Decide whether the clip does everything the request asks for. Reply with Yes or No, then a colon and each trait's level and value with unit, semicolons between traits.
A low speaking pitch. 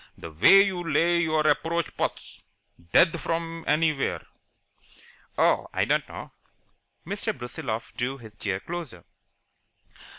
No: medium, 155 Hz